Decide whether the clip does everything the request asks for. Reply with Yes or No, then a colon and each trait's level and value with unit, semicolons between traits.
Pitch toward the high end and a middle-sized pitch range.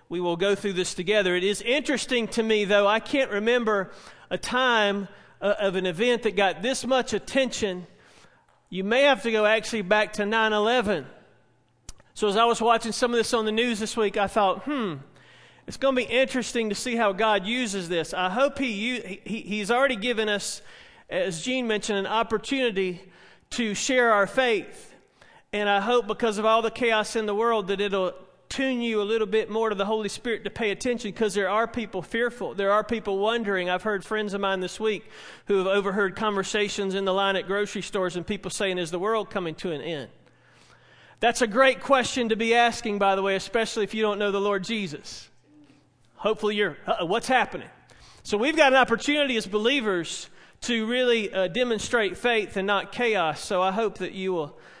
Yes: high, 210 Hz; average, 3.2 semitones